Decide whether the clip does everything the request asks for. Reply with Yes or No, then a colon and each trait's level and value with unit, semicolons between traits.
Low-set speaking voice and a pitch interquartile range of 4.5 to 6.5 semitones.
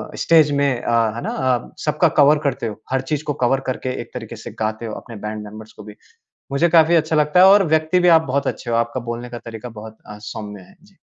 Yes: low, 125 Hz; average, 5.3 semitones